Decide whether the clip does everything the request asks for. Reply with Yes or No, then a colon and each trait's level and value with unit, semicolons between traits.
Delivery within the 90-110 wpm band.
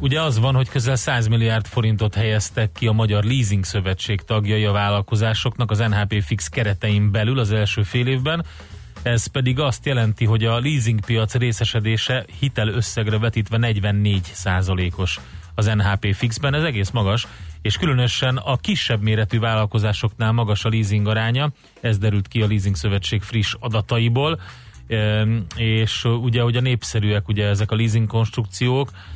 No: average, 150 wpm